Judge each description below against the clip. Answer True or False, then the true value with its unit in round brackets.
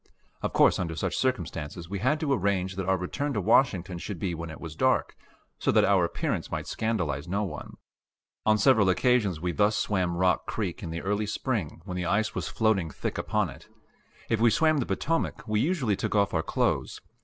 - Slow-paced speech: False (205 wpm)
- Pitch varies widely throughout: False (4.1 semitones)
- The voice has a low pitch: True (100 Hz)